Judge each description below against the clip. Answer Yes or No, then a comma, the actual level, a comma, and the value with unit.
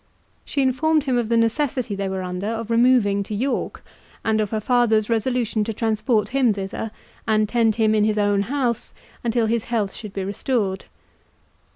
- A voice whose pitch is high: Yes, high, 225 Hz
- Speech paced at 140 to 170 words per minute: No, average, 180 wpm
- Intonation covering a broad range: No, average, 2.7 semitones